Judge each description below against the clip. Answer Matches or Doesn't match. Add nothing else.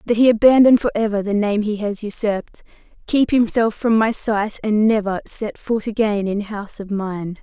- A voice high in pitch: Matches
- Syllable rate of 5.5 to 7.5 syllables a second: Doesn't match